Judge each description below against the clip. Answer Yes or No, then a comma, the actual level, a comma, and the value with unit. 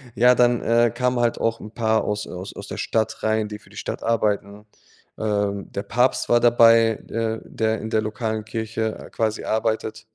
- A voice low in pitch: Yes, low, 110 Hz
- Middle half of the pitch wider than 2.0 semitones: No, narrow, 1.3 semitones